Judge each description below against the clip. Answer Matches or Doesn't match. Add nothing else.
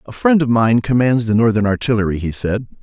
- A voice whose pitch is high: Doesn't match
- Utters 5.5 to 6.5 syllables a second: Matches